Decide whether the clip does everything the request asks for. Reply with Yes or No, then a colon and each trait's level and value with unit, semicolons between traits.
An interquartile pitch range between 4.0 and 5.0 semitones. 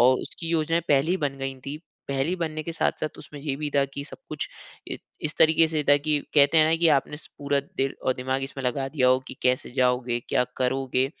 No: average, 2.8 semitones